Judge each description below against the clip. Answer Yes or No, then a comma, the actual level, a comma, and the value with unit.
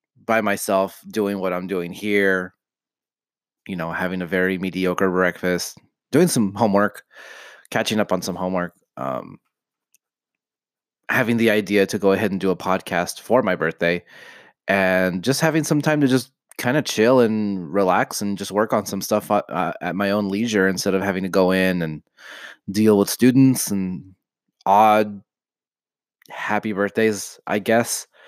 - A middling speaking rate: Yes, average, 160 wpm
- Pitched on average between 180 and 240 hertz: No, low, 100 Hz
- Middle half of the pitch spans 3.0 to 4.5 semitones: No, narrow, 2.4 semitones